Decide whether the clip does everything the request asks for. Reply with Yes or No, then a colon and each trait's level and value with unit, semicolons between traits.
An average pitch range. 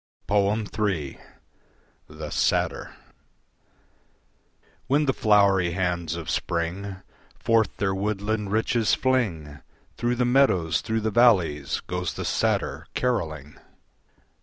Yes: average, 4.9 semitones